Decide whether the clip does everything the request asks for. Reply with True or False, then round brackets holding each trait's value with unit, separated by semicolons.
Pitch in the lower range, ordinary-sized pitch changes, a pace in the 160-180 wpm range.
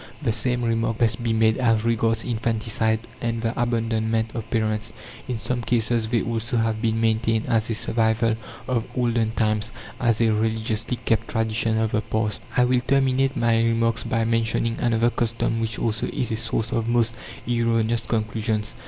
False (115 Hz; 0.9 semitones; 170 wpm)